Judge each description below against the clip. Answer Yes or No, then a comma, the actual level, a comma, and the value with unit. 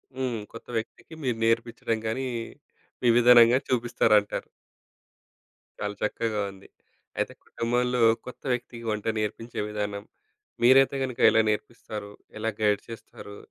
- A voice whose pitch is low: Yes, low, 115 Hz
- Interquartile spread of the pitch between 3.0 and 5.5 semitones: No, narrow, 2.5 semitones